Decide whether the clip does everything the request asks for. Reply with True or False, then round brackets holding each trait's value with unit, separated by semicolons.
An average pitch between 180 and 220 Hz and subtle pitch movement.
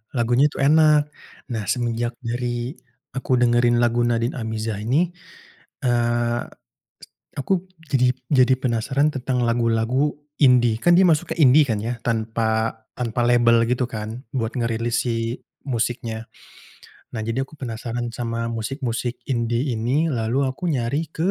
False (120 Hz; 1.9 semitones)